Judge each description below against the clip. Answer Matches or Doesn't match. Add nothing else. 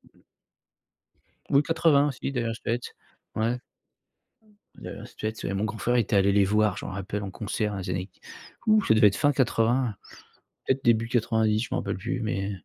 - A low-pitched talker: Matches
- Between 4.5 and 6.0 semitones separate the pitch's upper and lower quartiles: Doesn't match